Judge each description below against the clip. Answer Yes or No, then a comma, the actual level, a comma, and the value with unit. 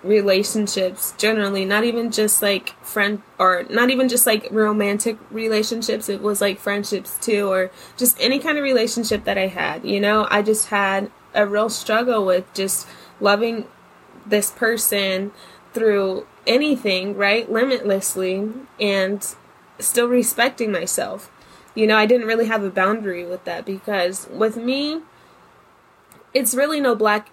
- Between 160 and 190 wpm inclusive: No, average, 145 wpm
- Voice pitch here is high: Yes, high, 210 Hz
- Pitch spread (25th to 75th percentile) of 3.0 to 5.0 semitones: No, narrow, 2.6 semitones